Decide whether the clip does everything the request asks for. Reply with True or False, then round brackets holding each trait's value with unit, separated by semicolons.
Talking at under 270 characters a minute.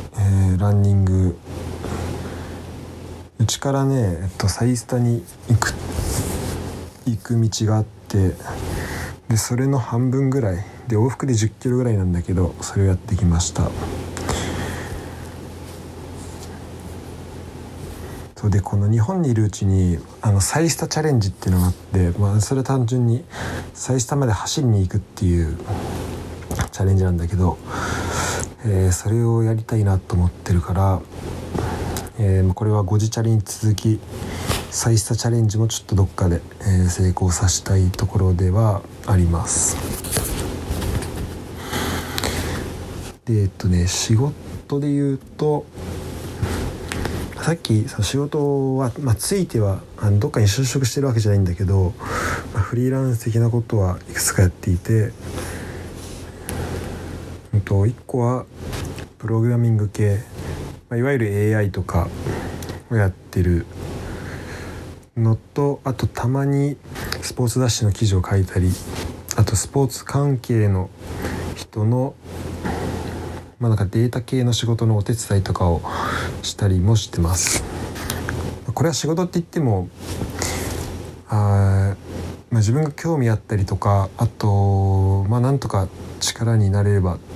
True (260 characters per minute)